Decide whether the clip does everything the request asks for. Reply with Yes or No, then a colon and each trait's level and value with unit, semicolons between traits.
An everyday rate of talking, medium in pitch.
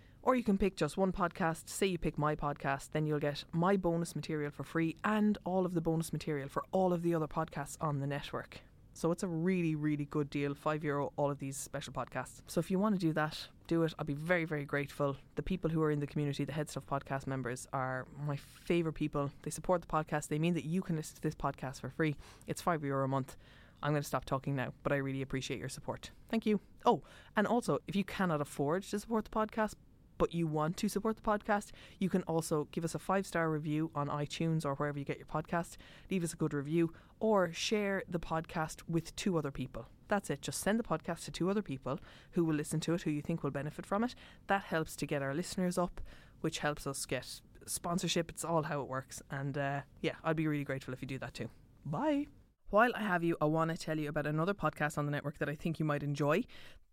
No: fast, 245 wpm; medium, 155 Hz